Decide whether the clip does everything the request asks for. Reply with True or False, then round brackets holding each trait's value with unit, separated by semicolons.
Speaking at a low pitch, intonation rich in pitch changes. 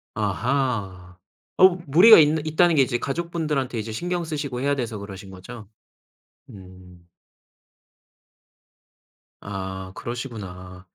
True (120 Hz; 7.5 semitones)